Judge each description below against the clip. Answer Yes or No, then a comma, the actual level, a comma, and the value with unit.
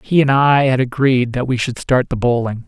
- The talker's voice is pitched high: No, low, 130 Hz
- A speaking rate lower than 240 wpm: No, fast, 245 wpm